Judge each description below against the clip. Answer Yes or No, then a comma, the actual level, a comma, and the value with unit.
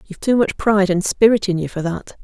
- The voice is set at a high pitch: Yes, high, 195 Hz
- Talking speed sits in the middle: No, fast, 270 wpm